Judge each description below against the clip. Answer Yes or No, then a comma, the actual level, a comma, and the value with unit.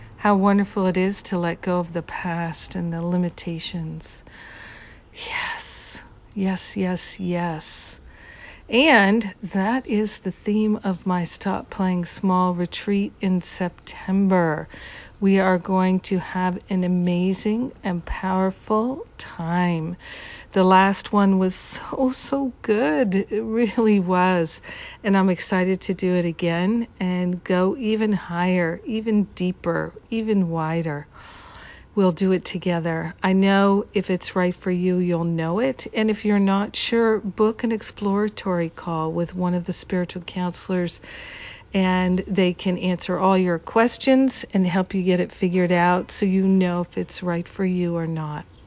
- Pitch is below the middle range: No, medium, 185 Hz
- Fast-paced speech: No, average, 145 wpm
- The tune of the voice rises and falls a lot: No, narrow, 2.4 semitones